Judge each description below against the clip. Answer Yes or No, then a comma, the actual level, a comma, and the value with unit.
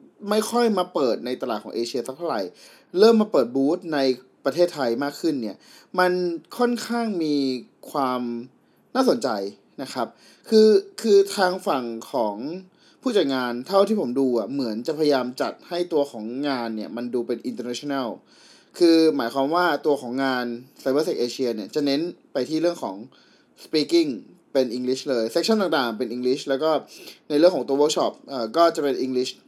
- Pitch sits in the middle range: Yes, medium, 145 Hz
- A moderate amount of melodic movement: No, wide, 7.6 semitones